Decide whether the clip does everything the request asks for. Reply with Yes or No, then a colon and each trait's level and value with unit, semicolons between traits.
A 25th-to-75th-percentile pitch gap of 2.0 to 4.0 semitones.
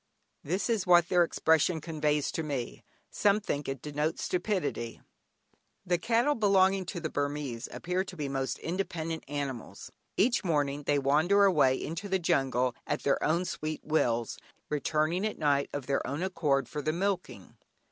No: average, 4.4 semitones